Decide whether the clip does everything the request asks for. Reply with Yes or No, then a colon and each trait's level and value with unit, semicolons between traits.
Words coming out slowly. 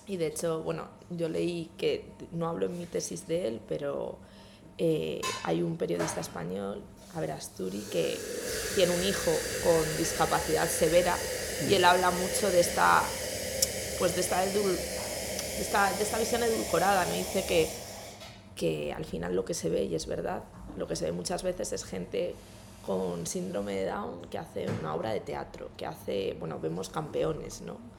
No: average, 175 wpm